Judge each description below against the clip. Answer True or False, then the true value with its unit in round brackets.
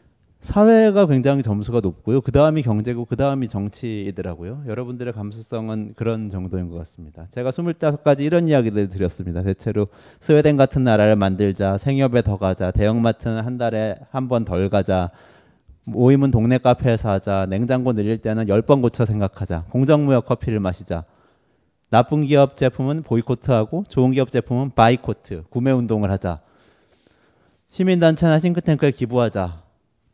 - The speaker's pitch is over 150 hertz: False (115 Hz)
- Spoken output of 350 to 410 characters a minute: True (355 characters per minute)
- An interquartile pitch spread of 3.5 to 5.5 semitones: True (5.1 semitones)